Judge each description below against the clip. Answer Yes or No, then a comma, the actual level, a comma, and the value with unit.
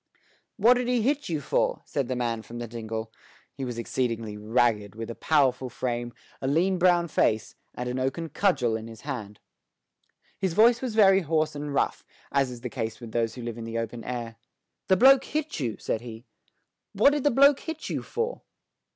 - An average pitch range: No, wide, 8.7 semitones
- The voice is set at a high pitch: No, low, 130 Hz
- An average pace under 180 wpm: No, average, 200 wpm